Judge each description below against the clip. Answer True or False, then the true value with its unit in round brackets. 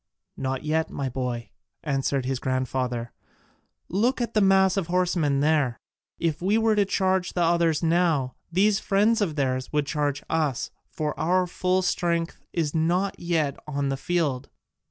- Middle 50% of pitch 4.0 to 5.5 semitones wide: True (4.9 semitones)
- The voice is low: False (160 Hz)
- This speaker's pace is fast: False (155 wpm)